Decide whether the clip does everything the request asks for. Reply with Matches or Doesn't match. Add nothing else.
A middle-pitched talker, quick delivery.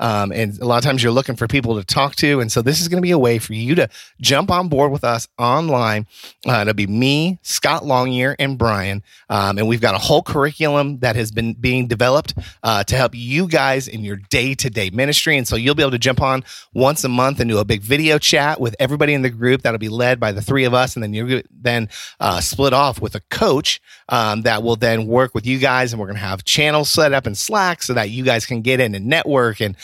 Doesn't match